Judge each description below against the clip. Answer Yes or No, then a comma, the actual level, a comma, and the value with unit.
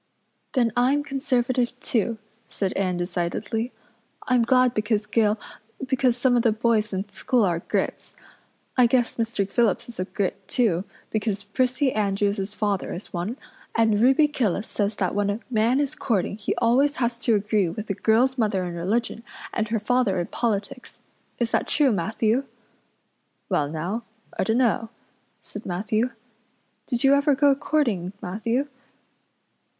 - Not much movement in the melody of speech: No, average, 3.7 semitones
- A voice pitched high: Yes, high, 225 Hz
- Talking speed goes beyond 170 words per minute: No, average, 155 wpm